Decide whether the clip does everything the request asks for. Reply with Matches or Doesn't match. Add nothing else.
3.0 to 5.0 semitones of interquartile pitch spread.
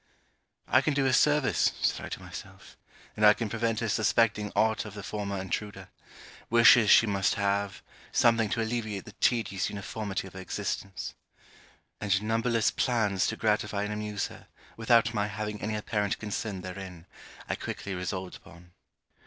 Doesn't match